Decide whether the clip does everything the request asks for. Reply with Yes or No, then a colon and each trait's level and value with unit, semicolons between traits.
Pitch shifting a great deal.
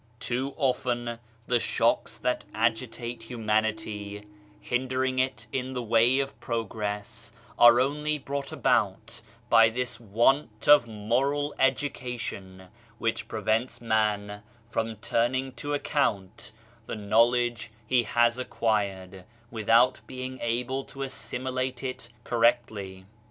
No: average, 2.8 semitones